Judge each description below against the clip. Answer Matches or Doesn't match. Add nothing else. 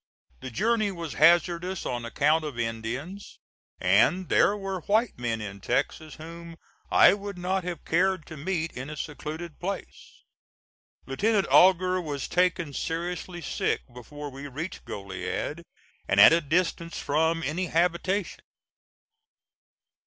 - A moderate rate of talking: Doesn't match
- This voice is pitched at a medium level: Matches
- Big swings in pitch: Doesn't match